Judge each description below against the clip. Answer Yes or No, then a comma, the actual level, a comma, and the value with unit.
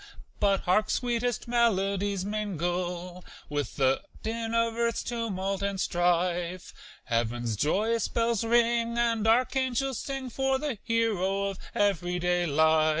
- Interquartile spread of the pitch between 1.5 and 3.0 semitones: No, average, 4.7 semitones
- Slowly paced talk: Yes, slow, 125 wpm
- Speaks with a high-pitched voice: Yes, high, 200 Hz